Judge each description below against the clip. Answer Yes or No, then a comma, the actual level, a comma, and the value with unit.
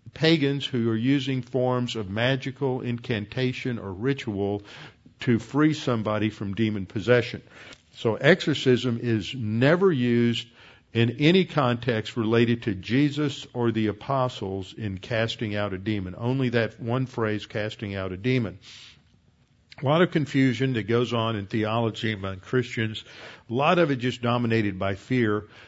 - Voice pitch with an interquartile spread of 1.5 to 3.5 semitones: Yes, average, 3.0 semitones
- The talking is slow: No, average, 145 wpm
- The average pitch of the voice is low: Yes, low, 120 Hz